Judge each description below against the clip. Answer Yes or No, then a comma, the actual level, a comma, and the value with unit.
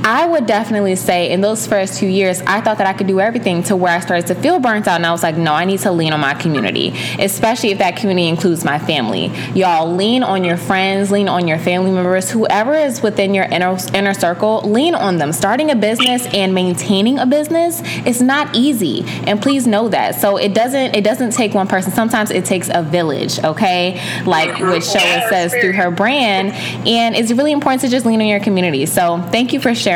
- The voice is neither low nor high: No, high, 200 Hz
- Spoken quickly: Yes, fast, 225 wpm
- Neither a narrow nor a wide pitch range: Yes, average, 4.2 semitones